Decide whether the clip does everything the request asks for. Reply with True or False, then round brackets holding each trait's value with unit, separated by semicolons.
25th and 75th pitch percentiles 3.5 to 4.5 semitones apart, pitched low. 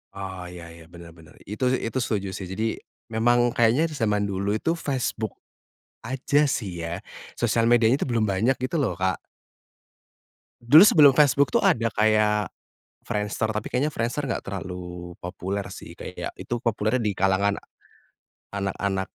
True (4.1 semitones; 105 Hz)